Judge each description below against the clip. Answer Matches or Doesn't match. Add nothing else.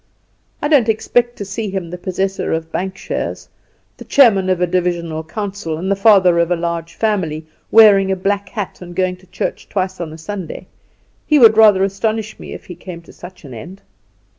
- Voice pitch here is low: Doesn't match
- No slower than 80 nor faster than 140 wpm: Doesn't match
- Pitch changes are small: Doesn't match